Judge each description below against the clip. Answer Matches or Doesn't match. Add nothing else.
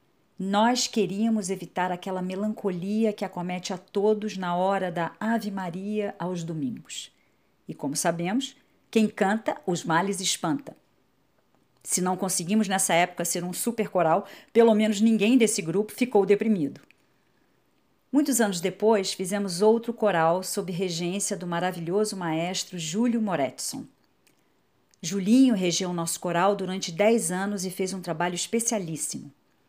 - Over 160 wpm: Doesn't match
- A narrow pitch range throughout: Doesn't match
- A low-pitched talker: Doesn't match